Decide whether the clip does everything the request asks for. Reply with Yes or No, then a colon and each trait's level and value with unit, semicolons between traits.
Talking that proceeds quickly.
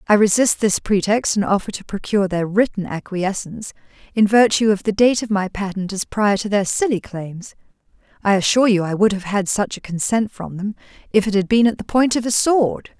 Yes: fast, 215 wpm